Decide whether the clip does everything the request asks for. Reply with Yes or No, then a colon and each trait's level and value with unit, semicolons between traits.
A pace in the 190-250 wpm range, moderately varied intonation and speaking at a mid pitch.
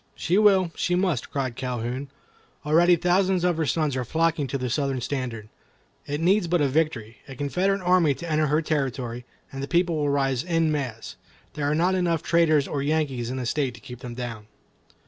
Yes: average, 195 wpm; average, 4.6 semitones; medium, 145 Hz